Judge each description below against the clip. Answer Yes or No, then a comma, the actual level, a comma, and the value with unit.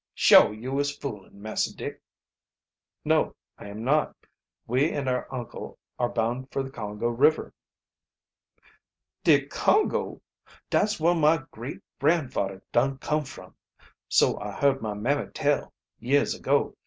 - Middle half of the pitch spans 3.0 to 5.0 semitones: Yes, average, 3.8 semitones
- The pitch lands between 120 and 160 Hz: Yes, low, 135 Hz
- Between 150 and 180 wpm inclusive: No, average, 140 wpm